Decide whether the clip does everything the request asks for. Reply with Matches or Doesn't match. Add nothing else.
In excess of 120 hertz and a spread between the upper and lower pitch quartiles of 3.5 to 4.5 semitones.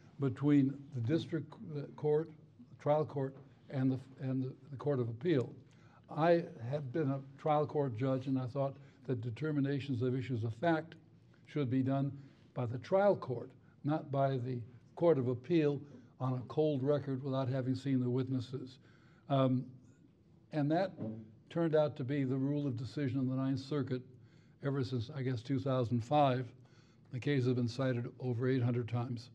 Doesn't match